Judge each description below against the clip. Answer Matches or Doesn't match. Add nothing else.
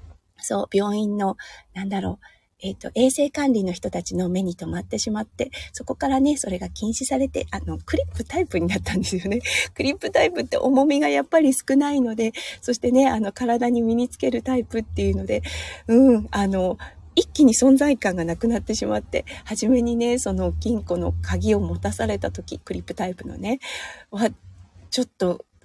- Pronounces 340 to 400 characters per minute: Matches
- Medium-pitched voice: Doesn't match